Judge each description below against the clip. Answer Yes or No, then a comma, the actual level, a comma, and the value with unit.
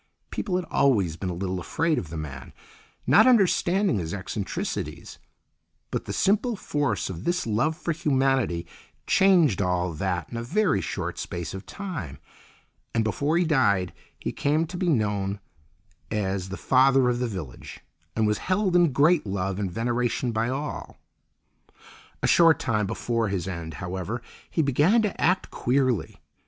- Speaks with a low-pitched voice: Yes, low, 120 Hz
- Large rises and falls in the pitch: Yes, wide, 9.0 semitones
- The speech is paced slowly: No, average, 160 wpm